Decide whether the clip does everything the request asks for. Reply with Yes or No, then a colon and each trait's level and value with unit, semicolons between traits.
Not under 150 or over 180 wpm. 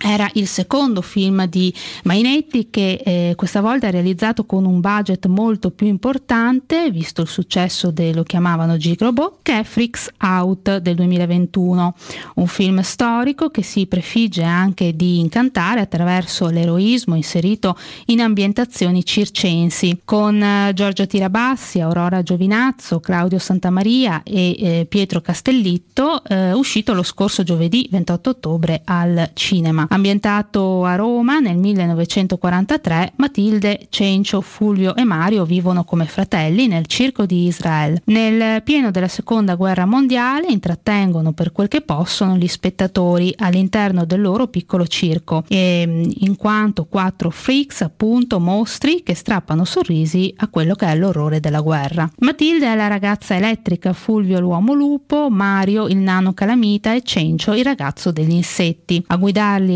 No: average, 140 wpm